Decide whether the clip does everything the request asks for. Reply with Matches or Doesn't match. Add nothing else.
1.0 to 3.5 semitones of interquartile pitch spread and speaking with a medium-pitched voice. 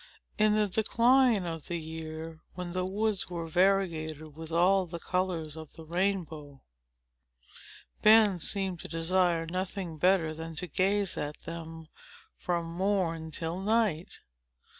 Matches